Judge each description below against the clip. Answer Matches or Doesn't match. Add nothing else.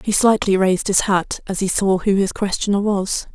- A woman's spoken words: Matches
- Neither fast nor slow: Doesn't match